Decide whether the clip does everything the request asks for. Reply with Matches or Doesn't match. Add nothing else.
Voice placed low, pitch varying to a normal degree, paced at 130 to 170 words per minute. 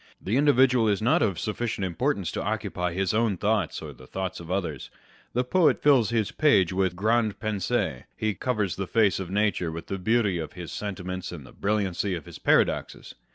Doesn't match